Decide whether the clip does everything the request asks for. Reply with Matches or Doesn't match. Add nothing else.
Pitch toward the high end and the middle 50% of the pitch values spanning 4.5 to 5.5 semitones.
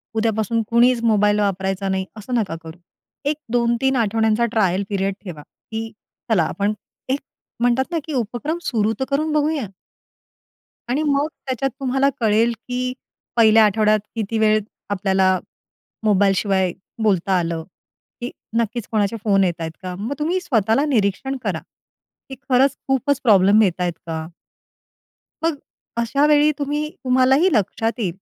Matches